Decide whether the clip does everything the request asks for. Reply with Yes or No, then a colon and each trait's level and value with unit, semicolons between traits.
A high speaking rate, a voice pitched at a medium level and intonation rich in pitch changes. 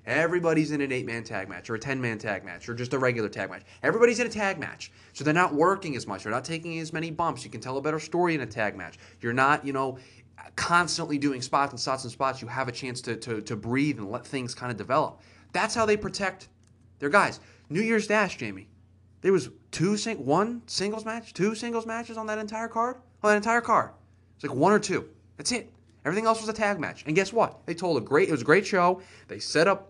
Yes: fast, 255 wpm; medium, 150 Hz; wide, 9.0 semitones